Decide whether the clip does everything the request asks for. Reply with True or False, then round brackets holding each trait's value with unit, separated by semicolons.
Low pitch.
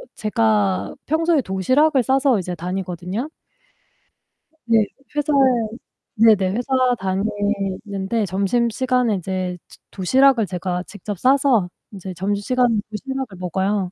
False (205 Hz)